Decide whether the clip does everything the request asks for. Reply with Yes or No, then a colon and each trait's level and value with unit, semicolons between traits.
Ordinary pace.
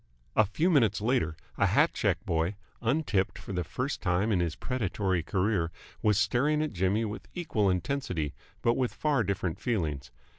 Yes: average, 165 wpm